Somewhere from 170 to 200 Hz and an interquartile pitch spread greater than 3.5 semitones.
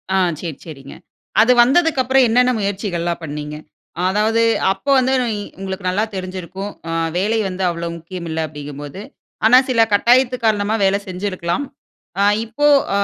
Yes: high, 195 Hz; average, 5.0 semitones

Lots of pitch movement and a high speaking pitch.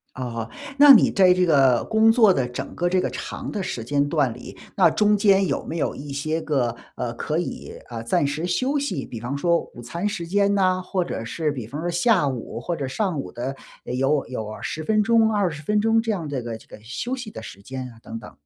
No: wide, 7.8 semitones; medium, 155 Hz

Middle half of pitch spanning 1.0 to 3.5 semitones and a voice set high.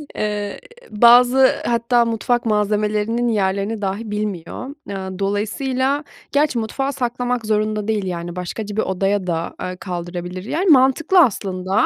No: average, 3.9 semitones; high, 215 Hz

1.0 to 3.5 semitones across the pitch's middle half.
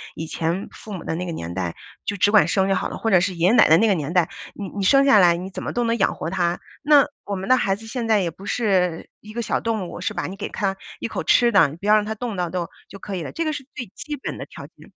No: average, 4.1 semitones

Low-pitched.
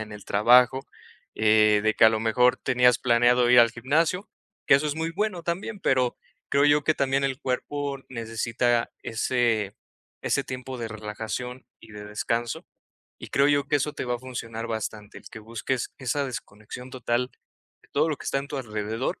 Yes: low, 125 Hz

